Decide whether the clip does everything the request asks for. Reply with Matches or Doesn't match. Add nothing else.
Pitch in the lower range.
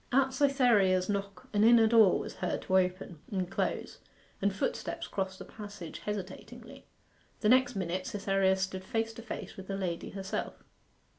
Doesn't match